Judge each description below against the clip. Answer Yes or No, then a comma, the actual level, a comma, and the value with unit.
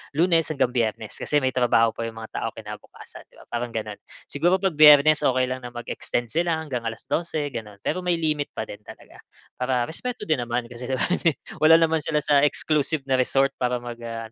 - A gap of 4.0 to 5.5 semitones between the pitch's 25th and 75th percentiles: Yes, average, 4.6 semitones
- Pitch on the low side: Yes, low, 130 Hz